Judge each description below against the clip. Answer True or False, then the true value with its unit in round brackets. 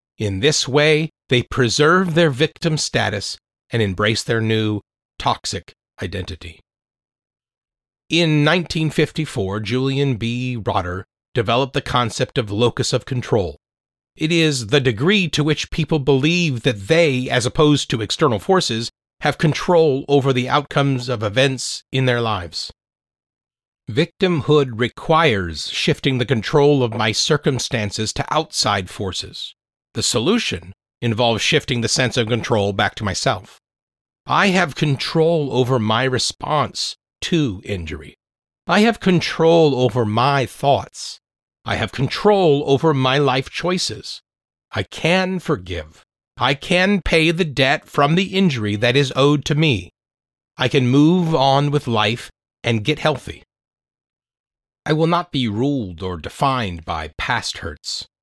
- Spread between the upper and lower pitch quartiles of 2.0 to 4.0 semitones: False (5.4 semitones)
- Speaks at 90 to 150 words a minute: True (135 wpm)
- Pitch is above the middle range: False (135 Hz)